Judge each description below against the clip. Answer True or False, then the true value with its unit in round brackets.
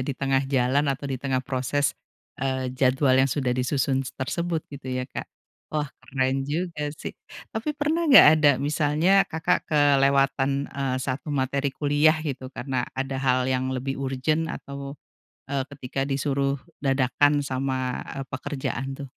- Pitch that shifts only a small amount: True (1.8 semitones)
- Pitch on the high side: False (135 Hz)